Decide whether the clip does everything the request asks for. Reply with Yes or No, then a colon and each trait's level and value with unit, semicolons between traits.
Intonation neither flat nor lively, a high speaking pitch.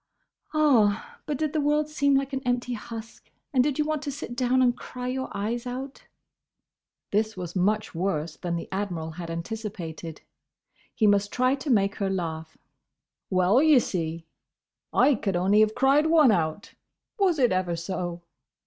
No: wide, 6.8 semitones; high, 215 Hz